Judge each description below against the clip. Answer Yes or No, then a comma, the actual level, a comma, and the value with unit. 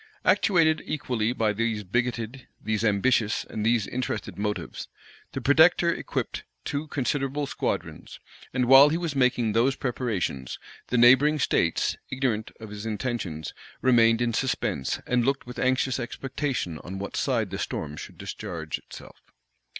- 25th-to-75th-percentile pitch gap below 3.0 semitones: No, average, 3.8 semitones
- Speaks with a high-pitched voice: No, low, 120 Hz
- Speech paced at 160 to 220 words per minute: No, average, 140 wpm